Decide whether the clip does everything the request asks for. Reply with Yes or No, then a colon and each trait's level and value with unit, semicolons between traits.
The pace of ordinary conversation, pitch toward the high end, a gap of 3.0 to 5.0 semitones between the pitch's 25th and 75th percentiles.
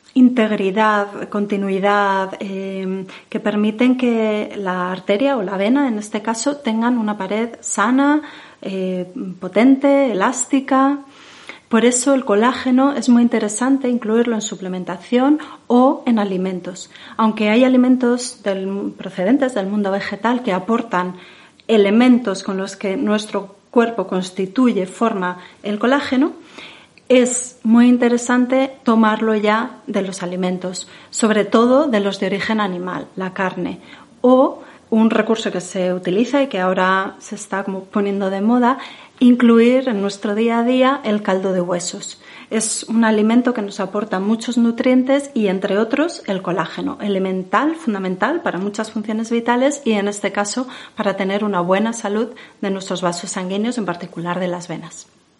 Yes: average, 145 wpm; high, 215 Hz; average, 4.2 semitones